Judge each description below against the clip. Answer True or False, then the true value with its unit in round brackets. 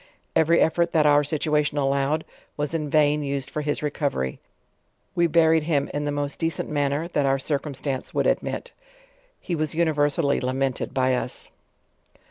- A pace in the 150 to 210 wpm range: True (160 wpm)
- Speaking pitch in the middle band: True (145 Hz)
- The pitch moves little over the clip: True (2.0 semitones)